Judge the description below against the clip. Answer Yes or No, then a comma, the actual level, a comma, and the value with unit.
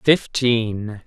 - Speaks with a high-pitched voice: No, low, 115 Hz